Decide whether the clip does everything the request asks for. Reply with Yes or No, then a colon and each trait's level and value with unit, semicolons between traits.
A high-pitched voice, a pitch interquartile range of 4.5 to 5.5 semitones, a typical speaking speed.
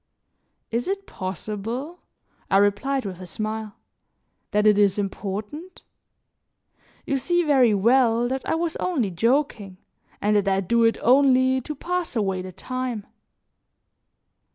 No: high, 230 Hz; average, 5.0 semitones; slow, 130 wpm